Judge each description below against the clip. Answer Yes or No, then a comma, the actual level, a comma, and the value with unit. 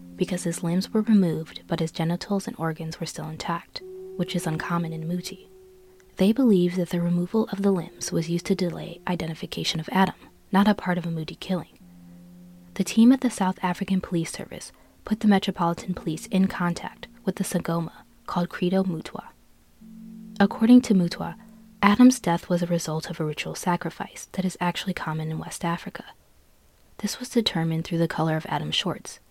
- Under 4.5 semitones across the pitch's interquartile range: Yes, average, 2.8 semitones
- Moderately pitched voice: Yes, medium, 180 Hz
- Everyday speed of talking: Yes, average, 180 wpm